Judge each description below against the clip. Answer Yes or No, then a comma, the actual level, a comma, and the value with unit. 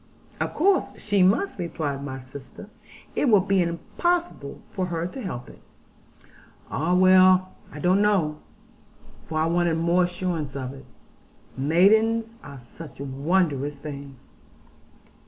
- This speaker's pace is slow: Yes, slow, 130 wpm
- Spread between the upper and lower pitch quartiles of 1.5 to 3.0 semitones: No, average, 5.1 semitones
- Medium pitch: Yes, medium, 170 Hz